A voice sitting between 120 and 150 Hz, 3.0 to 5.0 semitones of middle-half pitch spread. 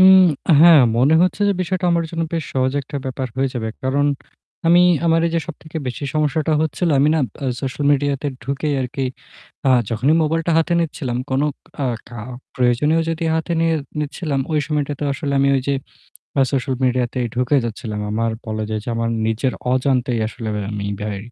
Yes: medium, 140 Hz; average, 4.2 semitones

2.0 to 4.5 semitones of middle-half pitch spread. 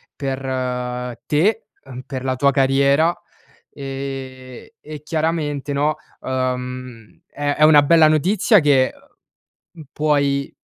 Yes: average, 2.7 semitones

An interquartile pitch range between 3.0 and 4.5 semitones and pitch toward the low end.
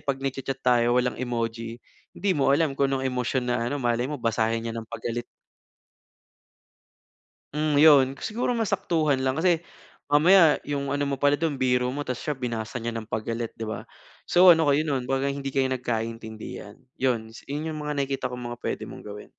Yes: average, 3.6 semitones; low, 130 Hz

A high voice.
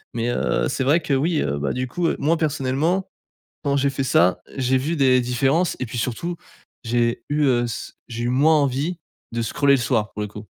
No: low, 130 Hz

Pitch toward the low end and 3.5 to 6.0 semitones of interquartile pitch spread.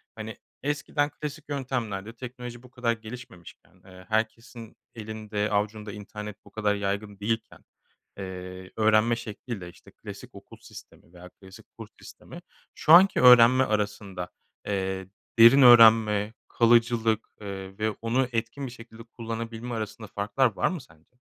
No: low, 110 Hz; average, 2.8 semitones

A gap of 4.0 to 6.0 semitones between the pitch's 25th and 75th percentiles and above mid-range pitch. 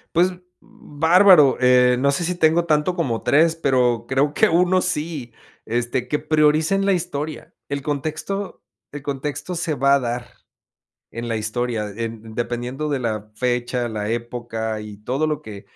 No: average, 4.8 semitones; medium, 140 Hz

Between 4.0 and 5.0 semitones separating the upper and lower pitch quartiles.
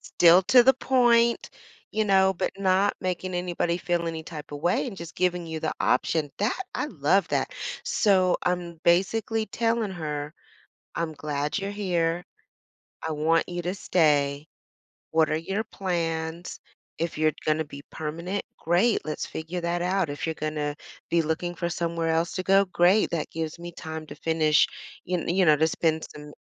No: average, 2.8 semitones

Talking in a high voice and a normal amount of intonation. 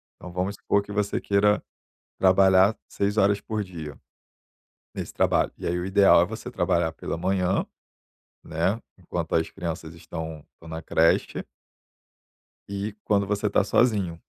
No: very low, 95 Hz; average, 3.4 semitones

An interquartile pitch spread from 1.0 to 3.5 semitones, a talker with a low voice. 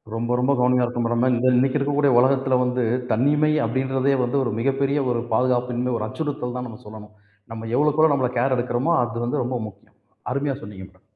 Yes: narrow, 2.5 semitones; low, 125 Hz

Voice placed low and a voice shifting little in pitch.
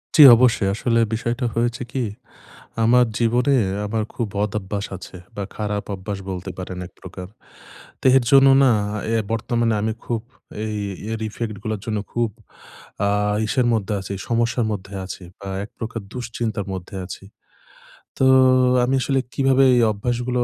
No: low, 115 Hz; average, 3.0 semitones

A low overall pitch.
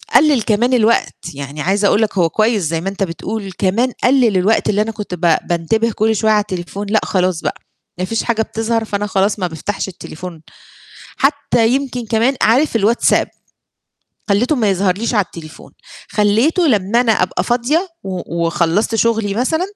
No: high, 210 Hz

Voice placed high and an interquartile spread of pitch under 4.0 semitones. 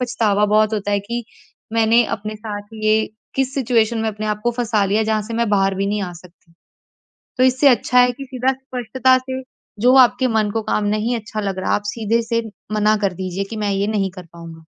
Yes: high, 215 Hz; average, 2.8 semitones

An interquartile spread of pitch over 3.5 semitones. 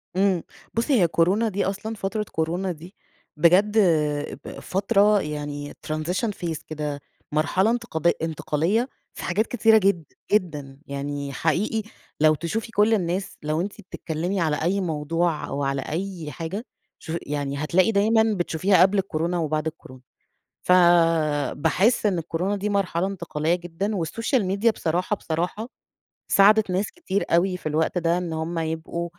Yes: average, 4.0 semitones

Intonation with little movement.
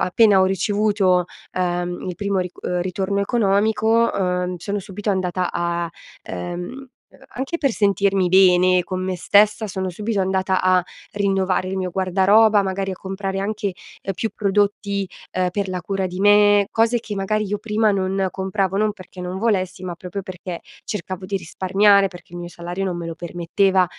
Yes: narrow, 2.1 semitones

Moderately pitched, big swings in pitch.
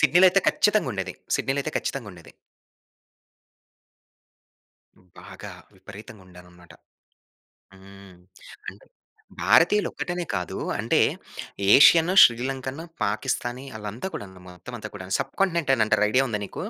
No: low, 115 Hz; wide, 7.3 semitones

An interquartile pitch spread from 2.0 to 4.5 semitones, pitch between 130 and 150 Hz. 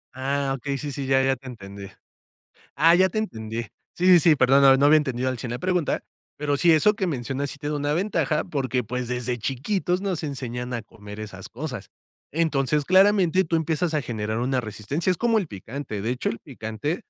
No: average, 4.9 semitones; medium, 140 Hz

